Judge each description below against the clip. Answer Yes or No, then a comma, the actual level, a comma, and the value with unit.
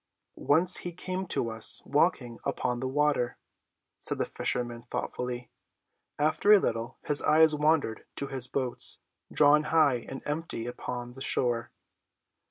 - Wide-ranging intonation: No, average, 4.1 semitones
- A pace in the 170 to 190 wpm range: No, average, 140 wpm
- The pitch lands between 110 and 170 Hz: Yes, low, 135 Hz